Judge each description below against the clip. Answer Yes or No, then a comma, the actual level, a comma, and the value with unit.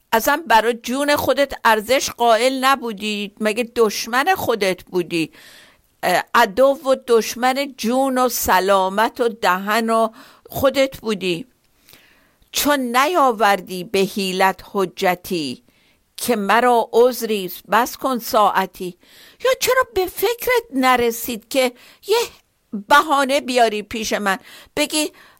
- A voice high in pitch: Yes, high, 235 Hz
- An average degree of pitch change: Yes, average, 4.3 semitones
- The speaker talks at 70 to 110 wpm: Yes, slow, 105 wpm